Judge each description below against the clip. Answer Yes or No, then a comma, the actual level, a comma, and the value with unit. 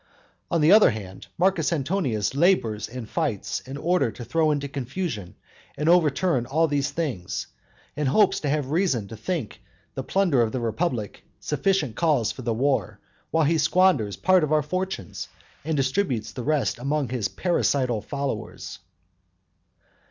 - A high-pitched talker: No, medium, 145 Hz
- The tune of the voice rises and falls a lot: Yes, wide, 6.0 semitones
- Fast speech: No, average, 155 wpm